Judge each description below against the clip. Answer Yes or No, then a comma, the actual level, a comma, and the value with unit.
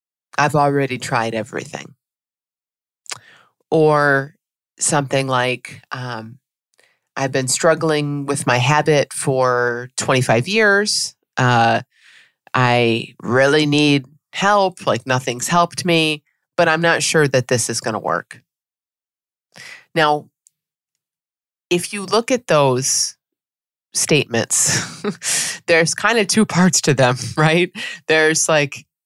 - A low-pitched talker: No, medium, 145 Hz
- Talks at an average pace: No, slow, 110 wpm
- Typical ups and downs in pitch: Yes, average, 4.3 semitones